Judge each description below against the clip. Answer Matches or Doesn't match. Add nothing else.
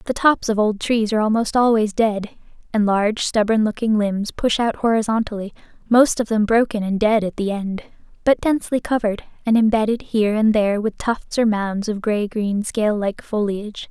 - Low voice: Doesn't match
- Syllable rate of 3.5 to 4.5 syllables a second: Doesn't match